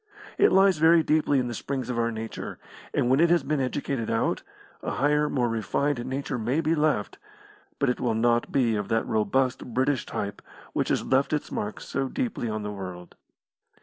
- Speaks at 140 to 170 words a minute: No, average, 195 wpm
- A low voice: Yes, low, 130 Hz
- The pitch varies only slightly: No, average, 4.4 semitones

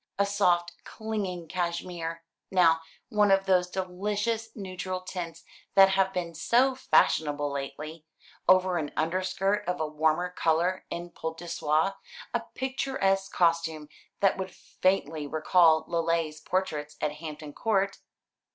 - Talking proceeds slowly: Yes, slow, 130 wpm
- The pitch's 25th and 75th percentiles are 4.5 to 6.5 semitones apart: No, average, 3.1 semitones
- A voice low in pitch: No, medium, 180 Hz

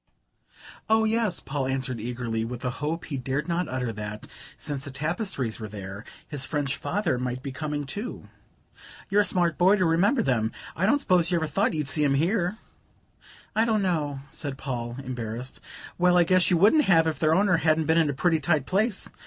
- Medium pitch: Yes, medium, 155 Hz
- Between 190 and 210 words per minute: Yes, average, 200 wpm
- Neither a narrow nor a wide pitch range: No, wide, 5.7 semitones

